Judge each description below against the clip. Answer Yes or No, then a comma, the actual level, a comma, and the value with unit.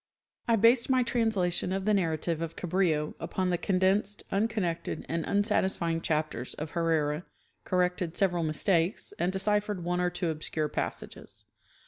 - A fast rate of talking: No, average, 140 wpm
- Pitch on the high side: No, medium, 180 Hz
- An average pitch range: Yes, average, 3.5 semitones